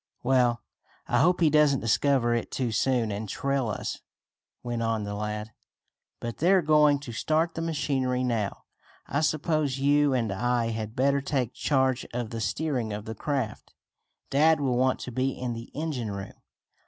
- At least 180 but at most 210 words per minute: No, average, 170 wpm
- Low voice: Yes, low, 130 Hz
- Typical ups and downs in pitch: Yes, average, 4.0 semitones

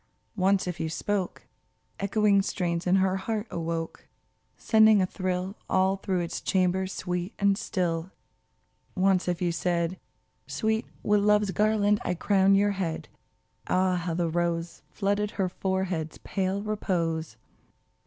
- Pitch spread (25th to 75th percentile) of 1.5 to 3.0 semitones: Yes, narrow, 2.5 semitones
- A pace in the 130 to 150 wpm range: Yes, slow, 135 wpm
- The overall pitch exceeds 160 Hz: Yes, medium, 185 Hz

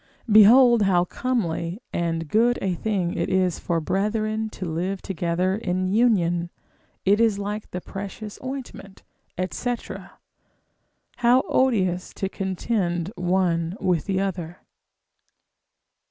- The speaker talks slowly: Yes, slow, 115 wpm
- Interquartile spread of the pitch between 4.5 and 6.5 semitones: No, average, 3.6 semitones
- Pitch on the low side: No, high, 190 Hz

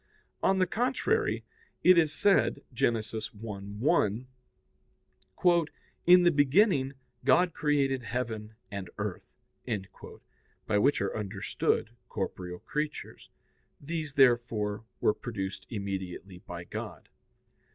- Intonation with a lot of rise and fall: Yes, wide, 7.1 semitones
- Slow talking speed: Yes, slow, 100 wpm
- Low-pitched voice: Yes, low, 120 Hz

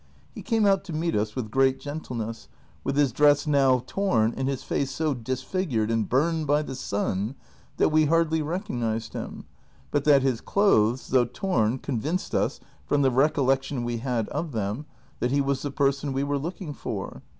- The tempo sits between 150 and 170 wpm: No, average, 185 wpm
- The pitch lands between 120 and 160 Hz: Yes, low, 135 Hz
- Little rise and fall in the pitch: No, average, 4.0 semitones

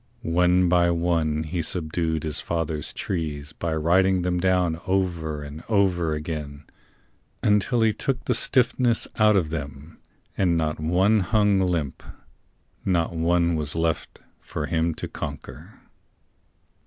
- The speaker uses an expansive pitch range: No, average, 3.0 semitones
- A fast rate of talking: No, slow, 135 wpm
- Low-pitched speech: Yes, very low, 85 Hz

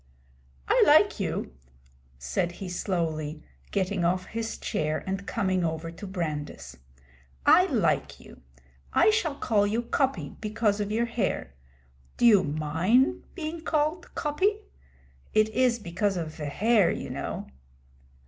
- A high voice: Yes, high, 200 Hz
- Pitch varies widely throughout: Yes, wide, 6.1 semitones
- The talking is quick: No, slow, 135 wpm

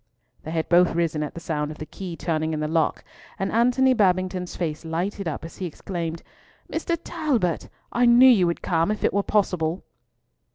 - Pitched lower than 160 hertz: No, medium, 175 Hz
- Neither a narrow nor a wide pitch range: Yes, average, 4.1 semitones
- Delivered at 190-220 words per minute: Yes, average, 195 wpm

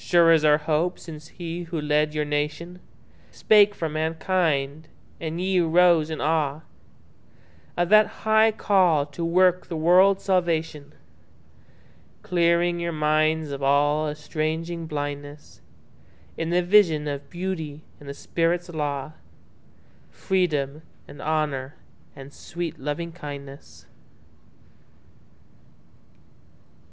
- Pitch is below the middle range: No, medium, 160 Hz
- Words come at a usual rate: No, slow, 100 wpm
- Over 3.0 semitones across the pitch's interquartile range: No, average, 2.7 semitones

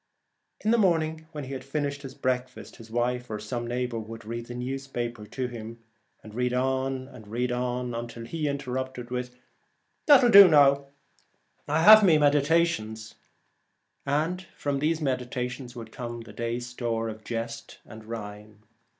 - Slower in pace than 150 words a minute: No, average, 160 wpm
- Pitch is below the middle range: Yes, low, 125 Hz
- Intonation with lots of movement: No, average, 3.3 semitones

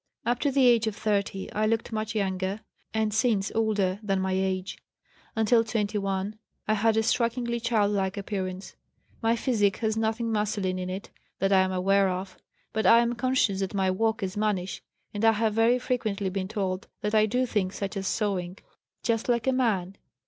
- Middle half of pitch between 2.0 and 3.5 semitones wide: Yes, average, 2.8 semitones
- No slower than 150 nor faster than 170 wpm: No, average, 190 wpm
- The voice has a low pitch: No, high, 210 Hz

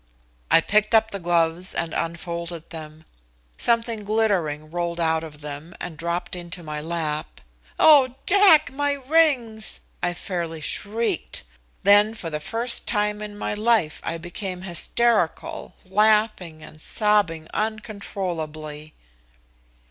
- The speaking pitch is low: No, medium, 180 Hz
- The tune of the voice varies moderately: Yes, average, 5.0 semitones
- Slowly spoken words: Yes, slow, 125 wpm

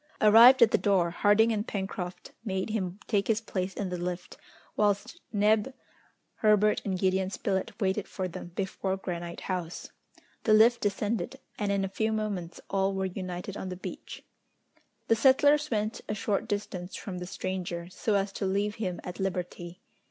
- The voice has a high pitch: Yes, high, 195 Hz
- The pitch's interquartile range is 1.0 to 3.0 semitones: Yes, narrow, 2.5 semitones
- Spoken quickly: No, average, 170 wpm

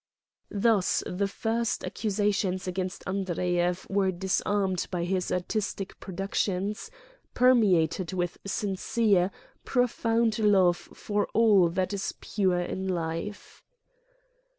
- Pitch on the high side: Yes, high, 195 Hz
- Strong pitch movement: No, narrow, 2.5 semitones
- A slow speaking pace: Yes, slow, 105 wpm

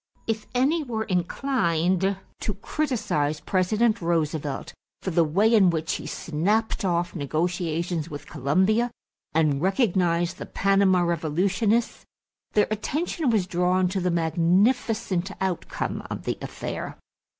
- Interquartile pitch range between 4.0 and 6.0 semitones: Yes, average, 4.4 semitones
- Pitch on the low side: No, medium, 185 Hz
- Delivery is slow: Yes, slow, 120 wpm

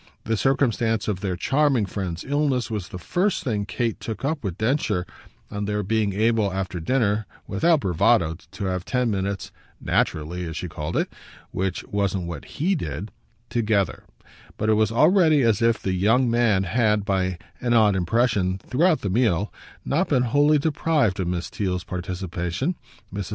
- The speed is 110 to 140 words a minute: No, average, 165 wpm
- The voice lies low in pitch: Yes, low, 105 Hz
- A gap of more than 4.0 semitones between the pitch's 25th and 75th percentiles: Yes, average, 4.9 semitones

